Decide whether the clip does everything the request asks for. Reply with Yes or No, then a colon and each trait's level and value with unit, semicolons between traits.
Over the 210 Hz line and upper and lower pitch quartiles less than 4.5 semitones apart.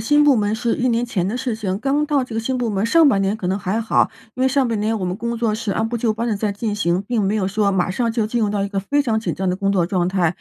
Yes: high, 220 Hz; average, 3.3 semitones